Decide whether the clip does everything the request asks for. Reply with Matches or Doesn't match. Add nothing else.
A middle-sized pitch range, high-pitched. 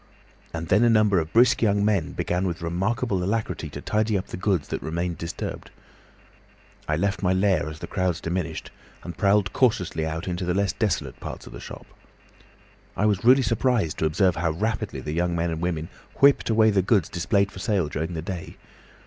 Doesn't match